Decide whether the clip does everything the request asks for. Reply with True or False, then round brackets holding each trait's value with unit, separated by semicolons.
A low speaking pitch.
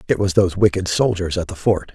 True (90 Hz)